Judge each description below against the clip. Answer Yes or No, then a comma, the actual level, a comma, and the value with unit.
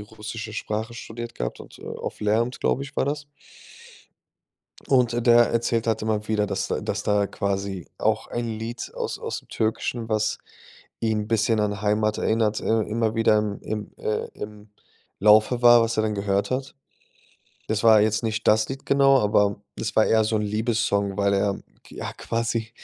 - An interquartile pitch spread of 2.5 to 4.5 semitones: No, narrow, 1.8 semitones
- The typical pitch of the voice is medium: No, low, 110 Hz